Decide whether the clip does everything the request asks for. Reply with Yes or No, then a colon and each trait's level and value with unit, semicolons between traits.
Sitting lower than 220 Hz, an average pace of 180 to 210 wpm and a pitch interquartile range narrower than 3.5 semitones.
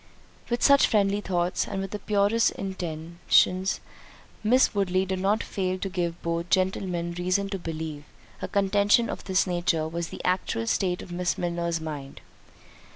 No: medium, 185 Hz; average, 155 wpm; narrow, 2.5 semitones